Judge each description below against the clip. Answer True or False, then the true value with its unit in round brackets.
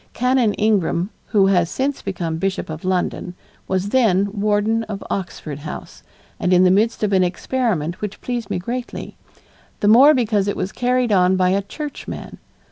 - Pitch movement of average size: True (4.0 semitones)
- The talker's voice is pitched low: False (200 Hz)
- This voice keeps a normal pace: True (170 wpm)